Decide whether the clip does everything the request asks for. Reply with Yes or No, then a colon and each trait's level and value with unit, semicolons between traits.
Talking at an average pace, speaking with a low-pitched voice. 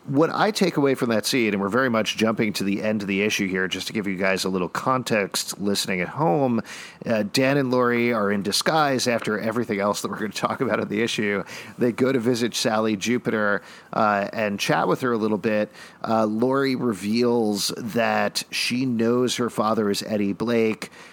No: fast, 210 wpm; low, 110 Hz